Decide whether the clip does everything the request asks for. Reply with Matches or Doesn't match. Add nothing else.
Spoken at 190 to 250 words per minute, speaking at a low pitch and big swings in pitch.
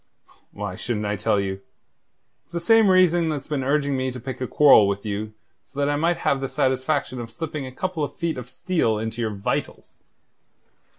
Matches